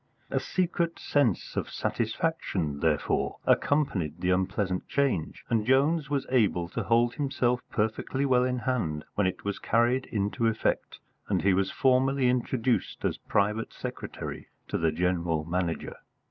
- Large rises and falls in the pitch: Yes, wide, 6.3 semitones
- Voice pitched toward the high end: No, low, 115 Hz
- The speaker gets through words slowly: No, average, 145 wpm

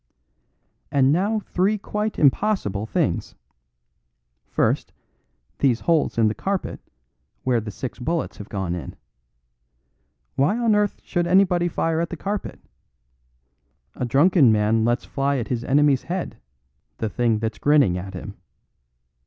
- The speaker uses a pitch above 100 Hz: Yes, medium, 140 Hz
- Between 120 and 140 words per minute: Yes, slow, 135 wpm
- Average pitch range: No, wide, 8.1 semitones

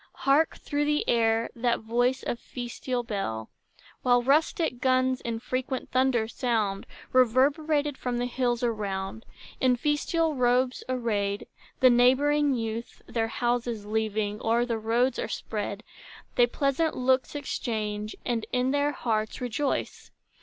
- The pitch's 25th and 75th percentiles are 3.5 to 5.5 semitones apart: No, average, 2.7 semitones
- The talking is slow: Yes, slow, 130 wpm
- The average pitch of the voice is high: Yes, high, 245 Hz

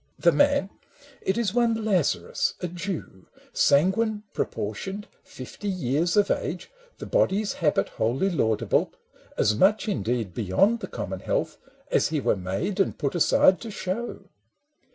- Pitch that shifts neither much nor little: No, wide, 8.1 semitones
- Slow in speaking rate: No, average, 145 wpm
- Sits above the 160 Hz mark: Yes, high, 190 Hz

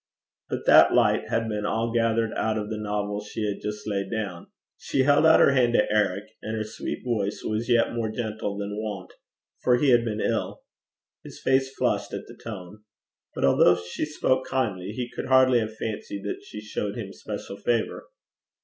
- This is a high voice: No, low, 110 Hz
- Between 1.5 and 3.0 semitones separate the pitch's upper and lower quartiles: Yes, narrow, 2.5 semitones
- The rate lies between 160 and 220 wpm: Yes, average, 195 wpm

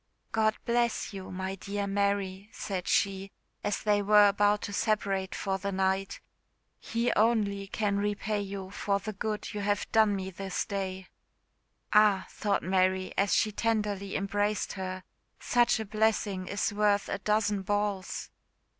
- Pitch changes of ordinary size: No, narrow, 1.5 semitones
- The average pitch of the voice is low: No, high, 200 Hz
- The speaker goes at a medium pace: Yes, average, 150 wpm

